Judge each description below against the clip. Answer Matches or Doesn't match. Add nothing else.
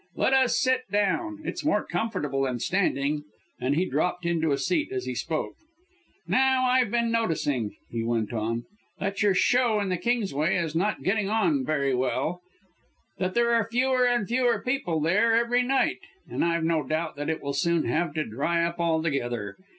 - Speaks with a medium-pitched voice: Matches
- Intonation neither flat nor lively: Doesn't match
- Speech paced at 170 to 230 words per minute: Matches